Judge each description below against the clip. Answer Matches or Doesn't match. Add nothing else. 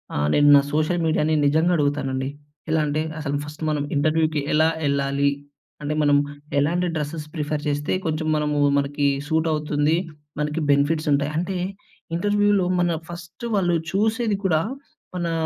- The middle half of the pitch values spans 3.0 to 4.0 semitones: Doesn't match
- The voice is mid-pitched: Matches